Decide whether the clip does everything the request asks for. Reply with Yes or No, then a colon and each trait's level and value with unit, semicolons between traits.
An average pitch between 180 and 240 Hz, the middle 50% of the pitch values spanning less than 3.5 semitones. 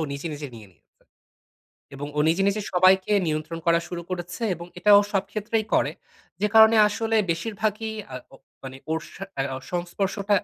No: medium, 185 Hz; average, 4.2 semitones